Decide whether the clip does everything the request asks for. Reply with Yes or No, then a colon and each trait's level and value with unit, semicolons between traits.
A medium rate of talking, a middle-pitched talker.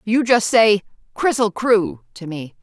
No: average, 160 wpm; high, 210 Hz